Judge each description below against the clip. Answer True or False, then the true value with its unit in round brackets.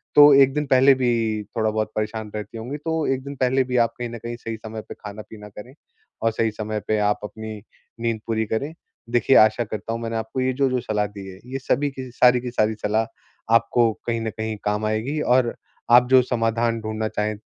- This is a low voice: True (115 Hz)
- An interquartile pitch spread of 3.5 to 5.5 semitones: False (2.6 semitones)